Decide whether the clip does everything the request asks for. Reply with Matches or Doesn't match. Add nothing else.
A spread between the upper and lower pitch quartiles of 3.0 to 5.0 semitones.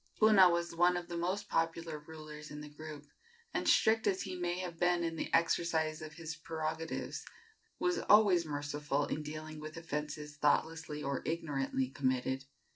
Doesn't match